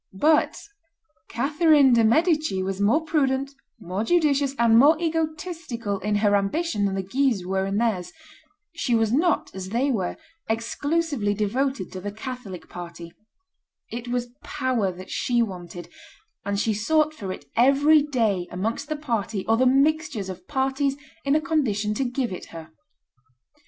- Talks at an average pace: Yes, average, 155 wpm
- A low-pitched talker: No, high, 235 Hz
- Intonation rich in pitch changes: Yes, wide, 6.2 semitones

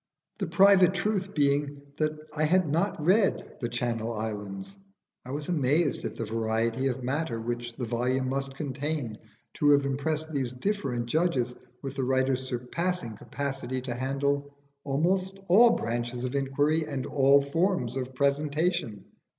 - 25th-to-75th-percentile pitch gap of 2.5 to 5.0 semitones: Yes, average, 4.1 semitones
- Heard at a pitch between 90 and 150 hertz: Yes, medium, 140 Hz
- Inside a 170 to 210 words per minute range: No, average, 150 wpm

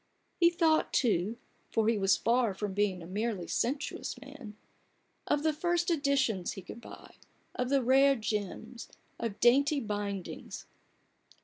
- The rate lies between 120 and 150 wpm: Yes, average, 140 wpm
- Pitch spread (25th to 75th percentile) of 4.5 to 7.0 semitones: Yes, average, 5.3 semitones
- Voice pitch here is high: Yes, high, 235 Hz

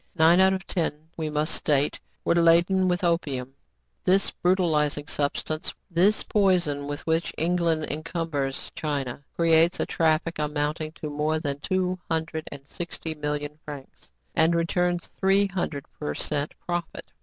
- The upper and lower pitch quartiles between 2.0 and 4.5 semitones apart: Yes, average, 2.8 semitones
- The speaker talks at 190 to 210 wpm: No, average, 145 wpm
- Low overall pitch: No, medium, 160 Hz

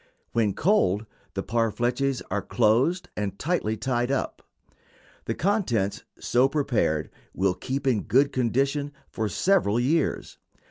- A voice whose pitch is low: Yes, low, 120 Hz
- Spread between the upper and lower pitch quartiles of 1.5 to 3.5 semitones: No, average, 4.7 semitones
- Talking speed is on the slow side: Yes, slow, 125 wpm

